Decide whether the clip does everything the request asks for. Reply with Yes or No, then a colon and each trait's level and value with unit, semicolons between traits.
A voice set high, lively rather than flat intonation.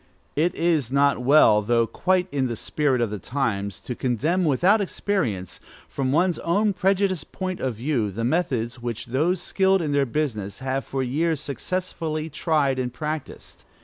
No: medium, 140 Hz; wide, 6.1 semitones